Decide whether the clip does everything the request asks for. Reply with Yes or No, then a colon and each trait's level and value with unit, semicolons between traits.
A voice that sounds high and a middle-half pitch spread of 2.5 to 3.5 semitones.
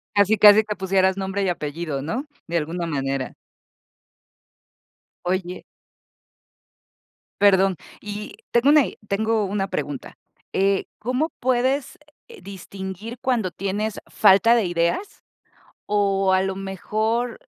Yes: high, 195 Hz; average, 2.8 semitones